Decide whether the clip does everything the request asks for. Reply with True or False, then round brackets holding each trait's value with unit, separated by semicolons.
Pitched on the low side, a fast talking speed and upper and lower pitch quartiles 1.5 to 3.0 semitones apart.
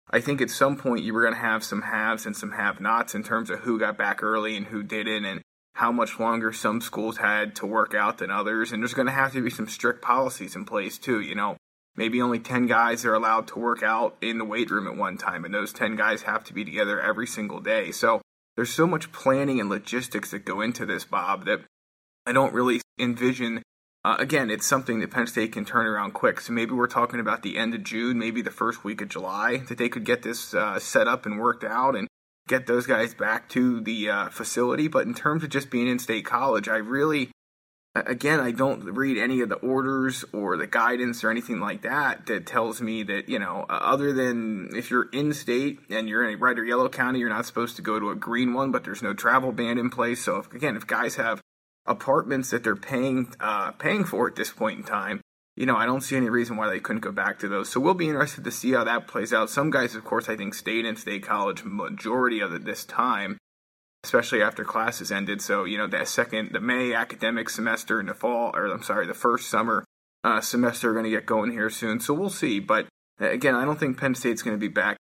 True (120 Hz; 245 wpm; 2.6 semitones)